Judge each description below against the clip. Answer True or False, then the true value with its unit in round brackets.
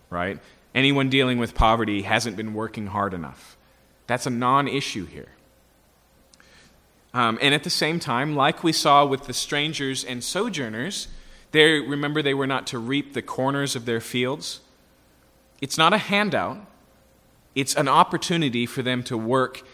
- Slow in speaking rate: False (155 wpm)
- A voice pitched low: True (130 Hz)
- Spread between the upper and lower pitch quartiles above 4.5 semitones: False (3.9 semitones)